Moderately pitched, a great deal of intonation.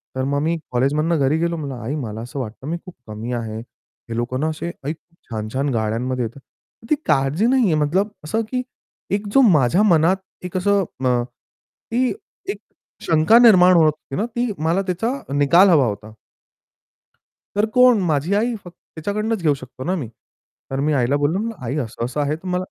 Yes: medium, 155 Hz; wide, 6.5 semitones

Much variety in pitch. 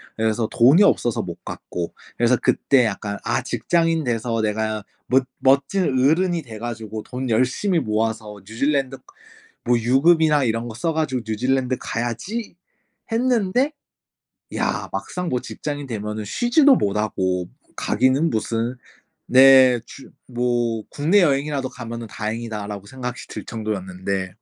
No: average, 4.5 semitones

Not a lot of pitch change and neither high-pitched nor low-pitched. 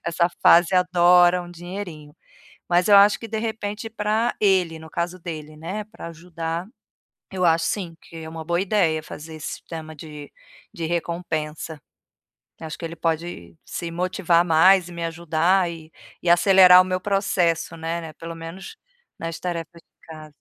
Yes: narrow, 2.2 semitones; medium, 170 Hz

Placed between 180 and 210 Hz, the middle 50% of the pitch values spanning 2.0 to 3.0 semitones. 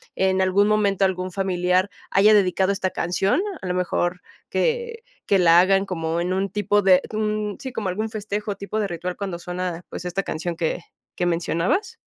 Yes: high, 190 Hz; narrow, 2.5 semitones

